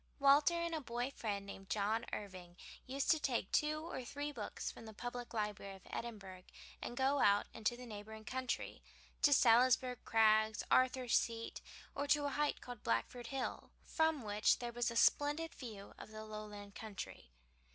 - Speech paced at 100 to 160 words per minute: No, average, 170 wpm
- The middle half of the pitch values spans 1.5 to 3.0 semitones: No, average, 4.4 semitones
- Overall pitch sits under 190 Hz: No, high, 235 Hz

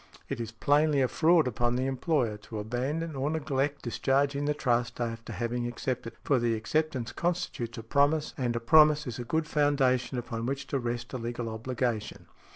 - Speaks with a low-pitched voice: Yes, low, 130 Hz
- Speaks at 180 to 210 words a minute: Yes, average, 185 wpm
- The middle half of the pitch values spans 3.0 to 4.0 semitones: Yes, average, 3.6 semitones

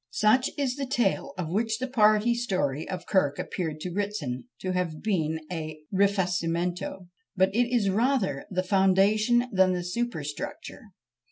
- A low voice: No, high, 190 Hz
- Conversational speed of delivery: Yes, average, 150 wpm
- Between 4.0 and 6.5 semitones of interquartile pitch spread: Yes, average, 4.3 semitones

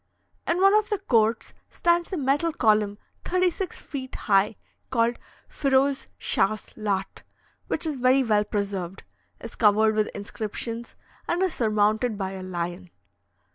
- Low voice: No, high, 225 Hz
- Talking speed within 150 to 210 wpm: No, average, 140 wpm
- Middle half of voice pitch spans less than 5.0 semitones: No, wide, 5.4 semitones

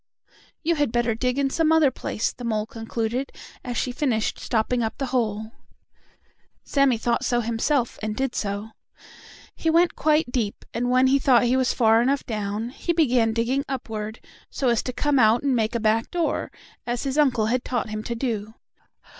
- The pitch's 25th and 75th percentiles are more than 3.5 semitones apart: No, average, 3.2 semitones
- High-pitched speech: Yes, high, 240 Hz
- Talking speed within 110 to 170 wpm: No, average, 190 wpm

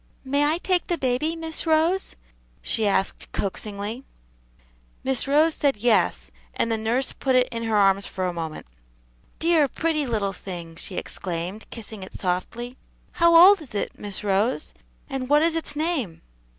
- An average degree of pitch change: No, wide, 7.5 semitones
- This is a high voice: Yes, high, 245 Hz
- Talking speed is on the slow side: No, average, 165 wpm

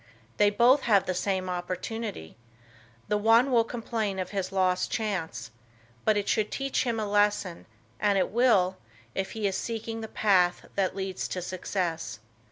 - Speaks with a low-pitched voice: No, high, 200 Hz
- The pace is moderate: Yes, average, 165 wpm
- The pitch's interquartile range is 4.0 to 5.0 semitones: No, average, 3.2 semitones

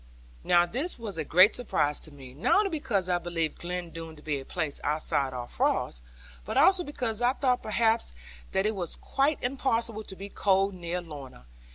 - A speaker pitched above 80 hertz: Yes, medium, 185 Hz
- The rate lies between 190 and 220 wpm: Yes, average, 195 wpm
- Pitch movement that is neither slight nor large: No, wide, 6.6 semitones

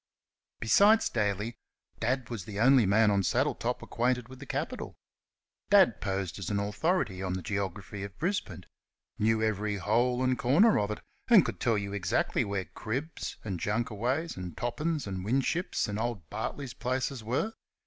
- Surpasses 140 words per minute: Yes, average, 160 wpm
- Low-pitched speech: Yes, low, 110 Hz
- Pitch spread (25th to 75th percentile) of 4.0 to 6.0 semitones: Yes, average, 4.3 semitones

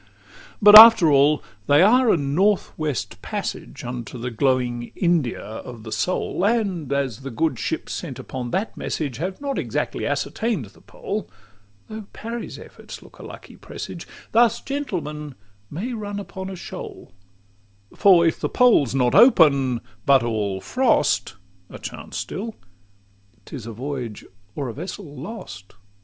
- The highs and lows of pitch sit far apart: Yes, wide, 8.4 semitones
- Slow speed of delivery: No, average, 150 wpm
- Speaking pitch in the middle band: Yes, medium, 150 Hz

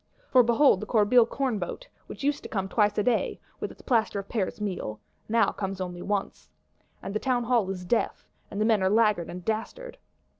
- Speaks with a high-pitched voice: Yes, high, 215 Hz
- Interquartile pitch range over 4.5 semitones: No, average, 3.7 semitones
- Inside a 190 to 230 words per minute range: Yes, average, 195 wpm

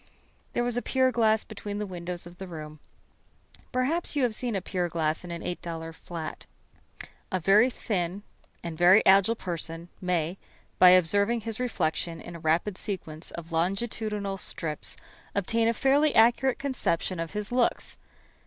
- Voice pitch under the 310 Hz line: Yes, high, 190 Hz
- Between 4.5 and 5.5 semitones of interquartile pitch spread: Yes, average, 5.1 semitones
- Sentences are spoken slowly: No, average, 160 wpm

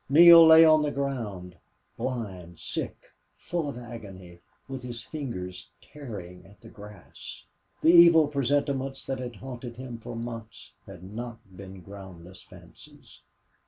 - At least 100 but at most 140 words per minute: Yes, slow, 135 wpm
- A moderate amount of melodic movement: No, wide, 6.2 semitones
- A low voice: Yes, low, 120 Hz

